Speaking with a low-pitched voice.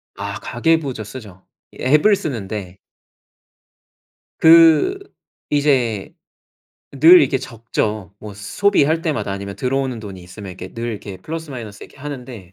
Yes: low, 120 Hz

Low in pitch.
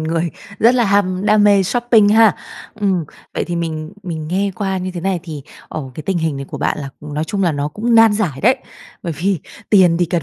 No: medium, 185 Hz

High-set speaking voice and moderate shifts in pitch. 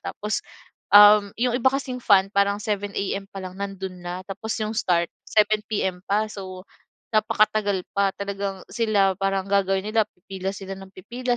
No: high, 200 Hz; narrow, 1.7 semitones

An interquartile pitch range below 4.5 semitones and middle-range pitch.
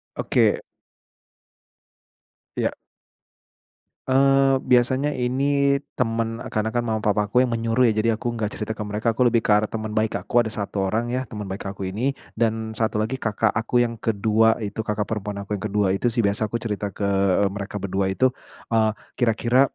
No: narrow, 2.5 semitones; low, 110 Hz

